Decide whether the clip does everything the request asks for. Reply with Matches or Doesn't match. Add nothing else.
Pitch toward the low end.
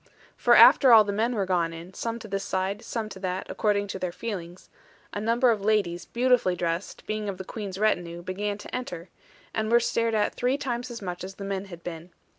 Doesn't match